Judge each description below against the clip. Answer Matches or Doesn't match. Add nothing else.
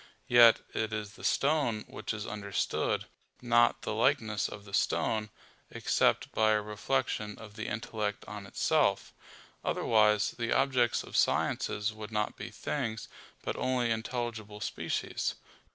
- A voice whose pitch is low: Matches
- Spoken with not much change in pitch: Matches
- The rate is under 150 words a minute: Matches